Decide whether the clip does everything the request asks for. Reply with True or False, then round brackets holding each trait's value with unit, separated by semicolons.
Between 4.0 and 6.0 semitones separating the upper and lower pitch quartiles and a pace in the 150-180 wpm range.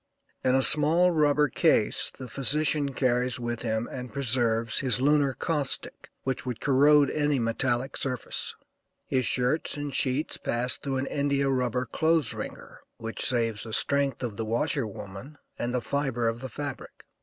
False (3.1 semitones; 160 wpm)